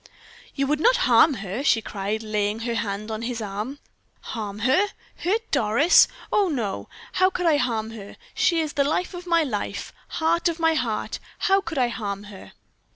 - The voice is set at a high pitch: Yes, very high, 250 Hz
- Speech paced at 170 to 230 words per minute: Yes, average, 180 wpm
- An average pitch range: No, wide, 7.5 semitones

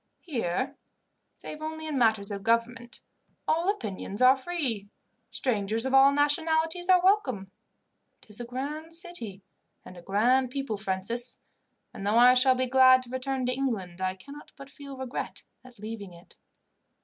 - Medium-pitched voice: No, very high, 255 Hz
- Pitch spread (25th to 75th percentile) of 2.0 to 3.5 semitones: No, average, 4.9 semitones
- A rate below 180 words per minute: Yes, average, 160 wpm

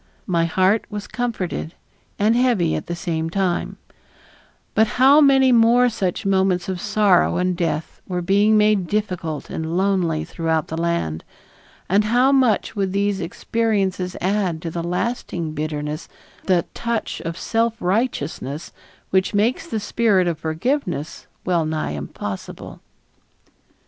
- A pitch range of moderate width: Yes, average, 4.4 semitones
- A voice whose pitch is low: No, medium, 185 Hz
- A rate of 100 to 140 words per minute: Yes, slow, 135 wpm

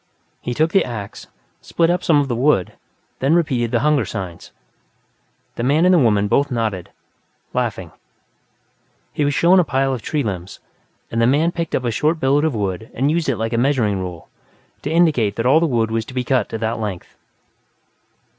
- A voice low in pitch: Yes, low, 125 Hz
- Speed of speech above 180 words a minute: Yes, average, 200 wpm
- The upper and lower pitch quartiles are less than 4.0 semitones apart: No, average, 5.3 semitones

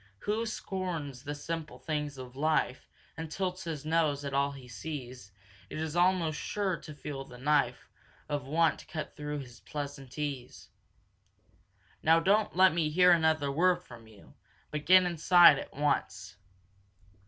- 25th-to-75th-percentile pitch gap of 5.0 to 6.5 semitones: No, average, 3.4 semitones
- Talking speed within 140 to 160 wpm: Yes, average, 150 wpm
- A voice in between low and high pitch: Yes, medium, 150 Hz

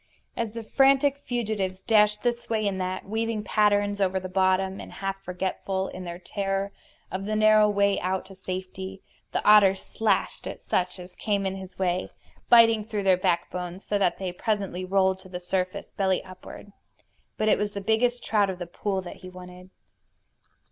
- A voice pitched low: No, high, 195 Hz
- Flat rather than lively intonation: Yes, narrow, 2.2 semitones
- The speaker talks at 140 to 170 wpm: No, average, 185 wpm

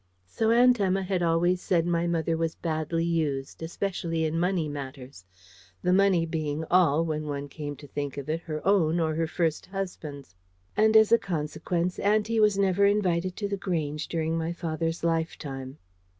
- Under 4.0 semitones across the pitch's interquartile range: Yes, average, 3.2 semitones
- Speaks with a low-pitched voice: No, medium, 165 Hz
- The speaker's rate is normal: Yes, average, 175 wpm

